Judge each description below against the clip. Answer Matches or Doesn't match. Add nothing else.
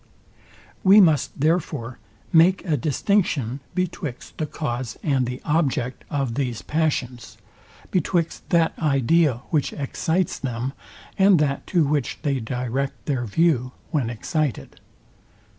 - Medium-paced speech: Doesn't match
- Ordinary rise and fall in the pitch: Matches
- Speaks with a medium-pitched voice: Matches